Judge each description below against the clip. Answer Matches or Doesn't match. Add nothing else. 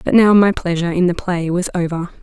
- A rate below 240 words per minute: Doesn't match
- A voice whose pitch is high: Doesn't match